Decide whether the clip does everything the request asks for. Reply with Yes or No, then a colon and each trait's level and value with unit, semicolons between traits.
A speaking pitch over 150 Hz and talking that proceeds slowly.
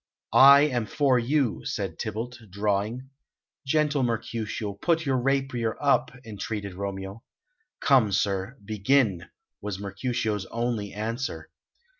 No: low, 115 Hz; slow, 110 wpm